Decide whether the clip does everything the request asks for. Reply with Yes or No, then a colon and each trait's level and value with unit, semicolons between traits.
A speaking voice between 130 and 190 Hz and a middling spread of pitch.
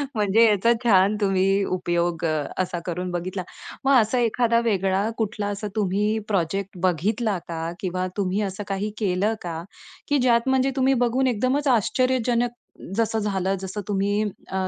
No: high, 205 Hz; average, 3.7 semitones